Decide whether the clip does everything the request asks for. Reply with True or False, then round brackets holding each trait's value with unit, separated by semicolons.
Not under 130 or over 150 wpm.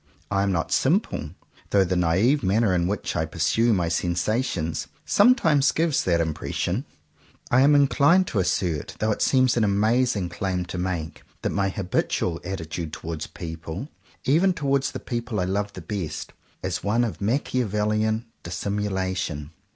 False (160 wpm)